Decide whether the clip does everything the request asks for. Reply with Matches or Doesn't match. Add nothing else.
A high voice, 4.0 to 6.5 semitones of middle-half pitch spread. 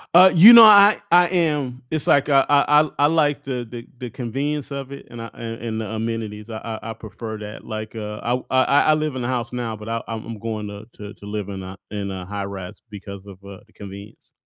Doesn't match